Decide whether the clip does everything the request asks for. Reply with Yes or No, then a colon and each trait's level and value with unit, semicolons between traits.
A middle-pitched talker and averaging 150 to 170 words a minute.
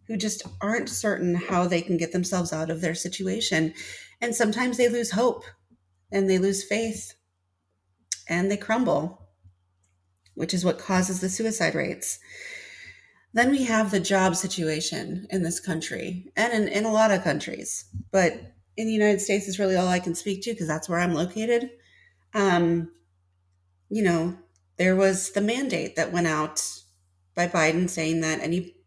Yes: medium, 175 Hz; average, 165 wpm